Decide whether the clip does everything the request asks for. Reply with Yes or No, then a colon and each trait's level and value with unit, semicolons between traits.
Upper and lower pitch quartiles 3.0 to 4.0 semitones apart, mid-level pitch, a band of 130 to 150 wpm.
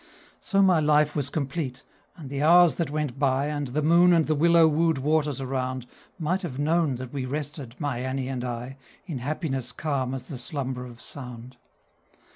No: average, 3.3 semitones; medium, 145 Hz; average, 185 wpm